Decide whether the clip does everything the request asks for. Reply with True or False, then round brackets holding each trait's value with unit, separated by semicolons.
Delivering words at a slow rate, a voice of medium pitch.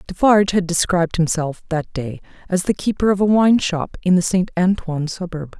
False (195 wpm; 180 Hz)